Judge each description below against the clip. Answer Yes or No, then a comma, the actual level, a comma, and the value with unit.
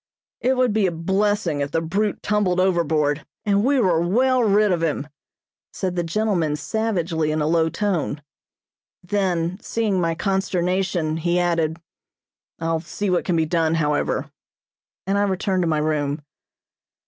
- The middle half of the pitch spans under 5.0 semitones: Yes, average, 3.9 semitones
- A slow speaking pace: No, average, 155 wpm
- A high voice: No, medium, 175 Hz